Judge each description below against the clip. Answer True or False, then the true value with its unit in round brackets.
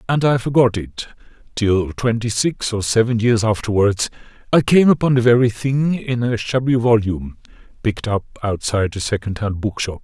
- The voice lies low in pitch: True (115 Hz)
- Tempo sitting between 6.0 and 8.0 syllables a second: False (5.1 syllables/s)